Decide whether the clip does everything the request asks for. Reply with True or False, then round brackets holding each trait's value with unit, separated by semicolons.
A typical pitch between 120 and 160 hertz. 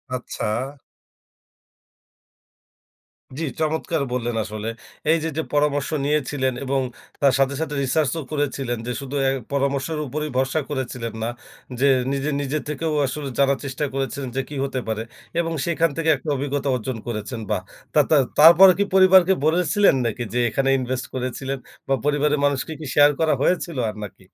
True (140 Hz)